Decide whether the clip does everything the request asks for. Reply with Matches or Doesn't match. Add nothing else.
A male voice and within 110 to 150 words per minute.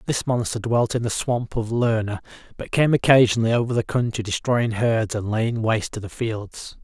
Doesn't match